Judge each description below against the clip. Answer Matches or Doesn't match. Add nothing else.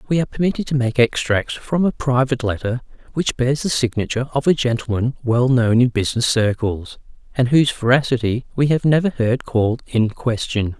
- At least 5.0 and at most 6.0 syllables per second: Matches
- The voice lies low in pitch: Matches